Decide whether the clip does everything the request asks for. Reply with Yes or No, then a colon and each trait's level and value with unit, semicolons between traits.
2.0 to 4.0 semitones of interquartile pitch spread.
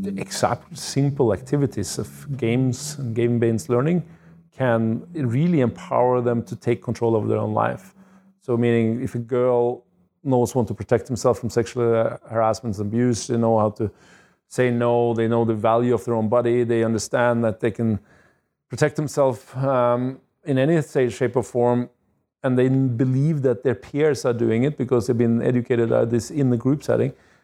Yes: narrow, 2.4 semitones